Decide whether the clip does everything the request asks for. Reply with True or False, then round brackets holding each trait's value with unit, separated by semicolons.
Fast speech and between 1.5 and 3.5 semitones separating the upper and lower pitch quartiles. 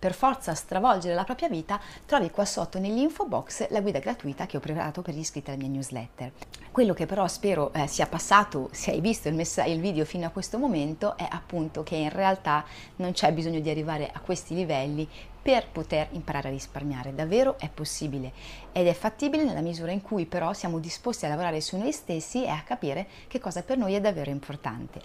False (200 wpm; 5.0 semitones)